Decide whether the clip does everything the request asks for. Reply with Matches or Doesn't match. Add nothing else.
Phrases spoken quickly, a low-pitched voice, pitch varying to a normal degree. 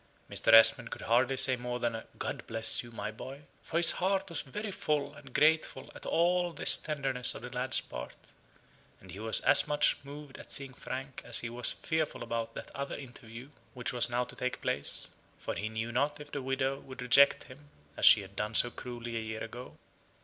Matches